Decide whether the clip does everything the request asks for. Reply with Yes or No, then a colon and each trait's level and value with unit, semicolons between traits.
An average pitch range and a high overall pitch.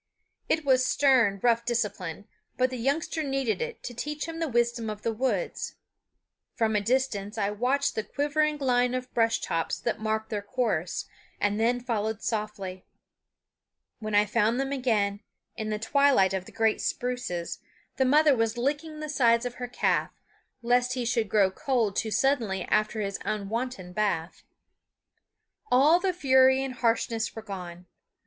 Yes: average, 3.8 semitones; high, 235 Hz